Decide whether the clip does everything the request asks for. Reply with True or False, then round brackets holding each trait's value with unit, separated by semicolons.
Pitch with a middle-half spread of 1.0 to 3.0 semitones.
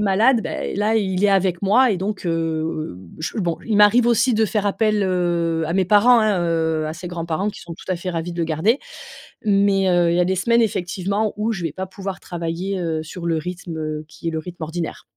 False (3.7 semitones)